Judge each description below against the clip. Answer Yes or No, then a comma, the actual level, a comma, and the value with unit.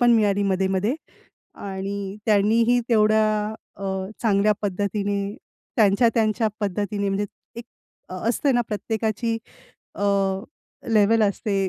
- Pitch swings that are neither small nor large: No, narrow, 1.9 semitones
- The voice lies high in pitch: Yes, high, 210 Hz